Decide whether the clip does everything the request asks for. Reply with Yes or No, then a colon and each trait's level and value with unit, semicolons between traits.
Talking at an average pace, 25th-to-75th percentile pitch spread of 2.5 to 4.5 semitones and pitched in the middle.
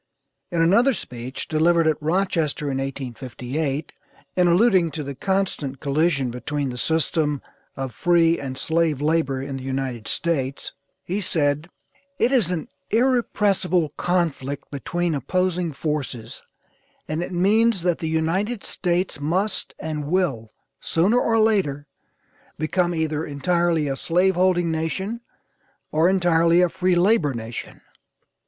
No: slow, 130 wpm; average, 4.2 semitones; medium, 165 Hz